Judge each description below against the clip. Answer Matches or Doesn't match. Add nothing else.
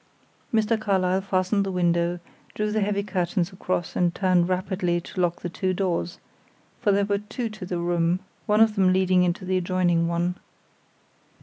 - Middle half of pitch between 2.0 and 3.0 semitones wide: Matches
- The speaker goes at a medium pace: Matches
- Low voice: Doesn't match